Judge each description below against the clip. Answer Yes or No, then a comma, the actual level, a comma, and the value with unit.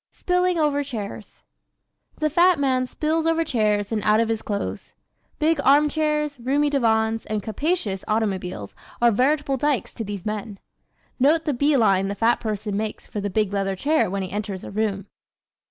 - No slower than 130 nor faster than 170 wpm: No, average, 180 wpm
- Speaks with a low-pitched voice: No, high, 230 Hz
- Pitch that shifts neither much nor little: No, wide, 6.3 semitones